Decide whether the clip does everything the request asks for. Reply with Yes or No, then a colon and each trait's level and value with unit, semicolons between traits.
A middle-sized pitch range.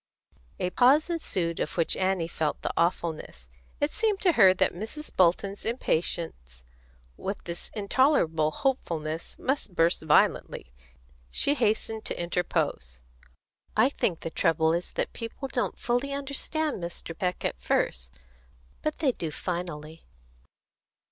No: wide, 8.1 semitones